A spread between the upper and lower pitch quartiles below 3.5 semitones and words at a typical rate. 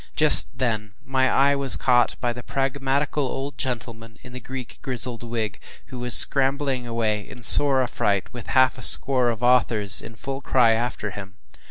Yes: average, 2.7 semitones; average, 175 wpm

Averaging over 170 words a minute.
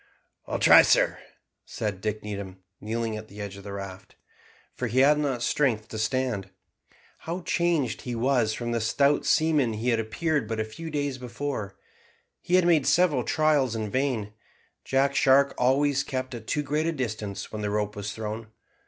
Yes: average, 180 wpm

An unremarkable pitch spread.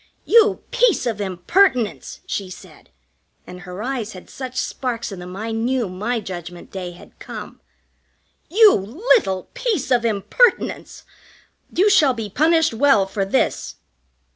No: wide, 7.8 semitones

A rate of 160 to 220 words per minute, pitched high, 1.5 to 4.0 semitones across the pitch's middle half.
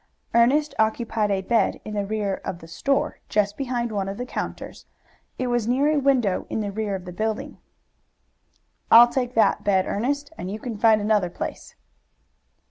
Yes: average, 180 wpm; high, 220 Hz; average, 3.5 semitones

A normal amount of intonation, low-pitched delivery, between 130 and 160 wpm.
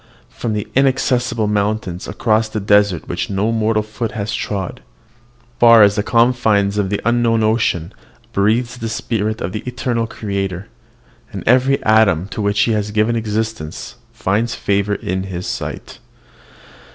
No: narrow, 2.3 semitones; low, 110 Hz; average, 150 wpm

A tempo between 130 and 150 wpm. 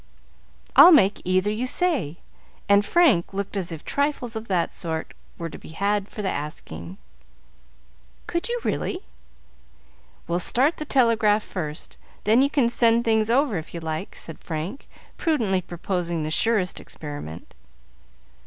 Yes: average, 145 wpm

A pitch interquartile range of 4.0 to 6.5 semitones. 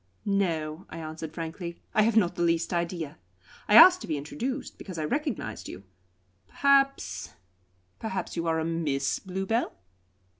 Yes: average, 5.1 semitones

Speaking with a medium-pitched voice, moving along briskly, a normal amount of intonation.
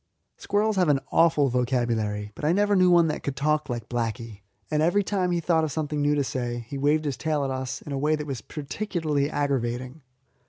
Yes: medium, 145 Hz; fast, 220 wpm; average, 4.2 semitones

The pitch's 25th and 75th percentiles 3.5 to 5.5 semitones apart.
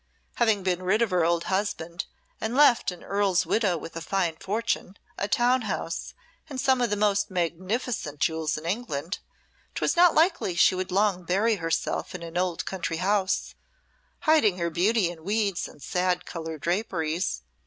Yes: average, 4.0 semitones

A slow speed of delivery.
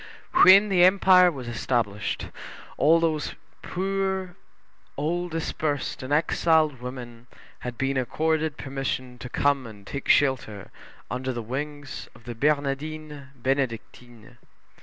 Yes: slow, 115 wpm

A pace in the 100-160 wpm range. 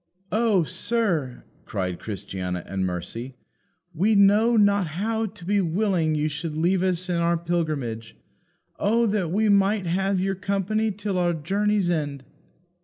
Yes: average, 145 wpm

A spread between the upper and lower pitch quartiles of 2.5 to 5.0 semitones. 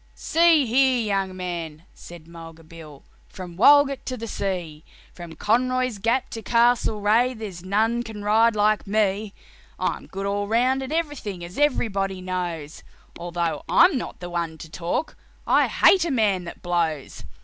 No: wide, 5.6 semitones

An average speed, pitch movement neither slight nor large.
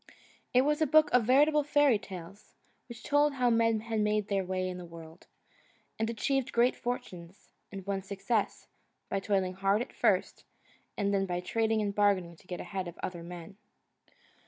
Yes: average, 180 wpm; average, 4.4 semitones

